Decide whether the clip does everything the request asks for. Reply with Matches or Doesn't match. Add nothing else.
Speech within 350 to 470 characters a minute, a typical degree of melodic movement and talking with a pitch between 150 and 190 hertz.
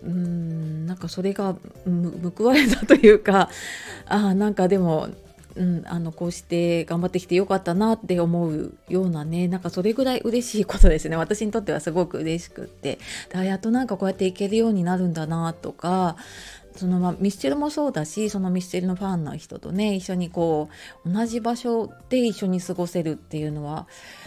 Matches